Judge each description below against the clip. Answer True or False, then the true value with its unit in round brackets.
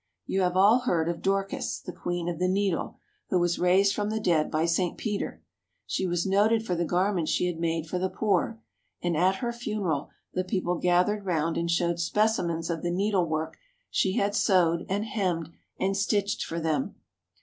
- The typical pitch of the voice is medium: True (180 Hz)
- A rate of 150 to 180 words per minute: False (190 wpm)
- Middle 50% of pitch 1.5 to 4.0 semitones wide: True (2.9 semitones)